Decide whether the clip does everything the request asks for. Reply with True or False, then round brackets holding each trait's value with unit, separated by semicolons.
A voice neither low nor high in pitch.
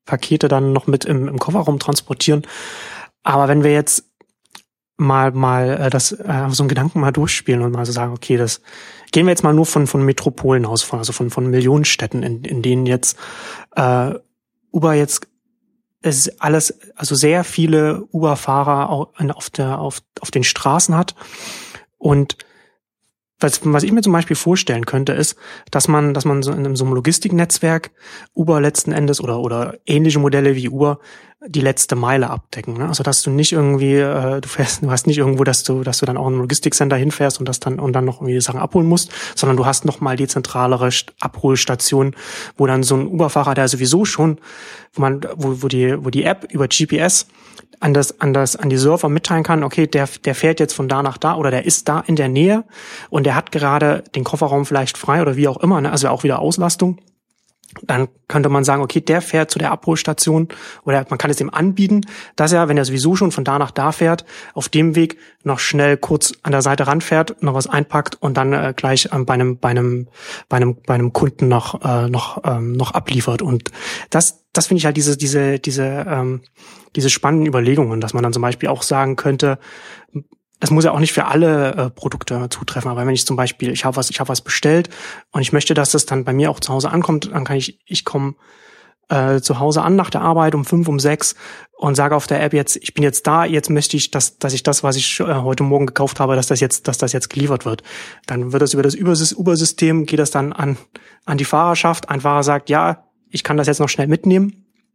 True (145 Hz)